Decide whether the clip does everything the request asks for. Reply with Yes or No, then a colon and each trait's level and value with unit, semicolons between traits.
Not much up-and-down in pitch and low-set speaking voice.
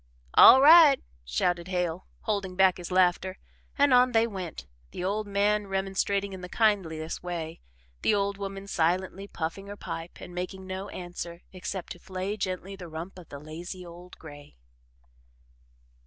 No: narrow, 2.3 semitones; medium, 185 Hz